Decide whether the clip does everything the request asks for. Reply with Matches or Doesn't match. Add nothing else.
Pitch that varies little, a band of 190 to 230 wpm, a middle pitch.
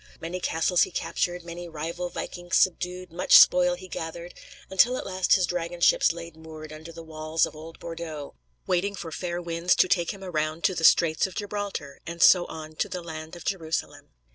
Matches